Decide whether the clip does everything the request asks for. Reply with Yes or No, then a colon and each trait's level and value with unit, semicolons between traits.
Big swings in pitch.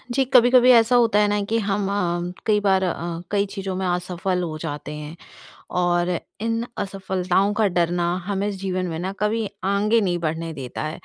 No: average, 3.0 semitones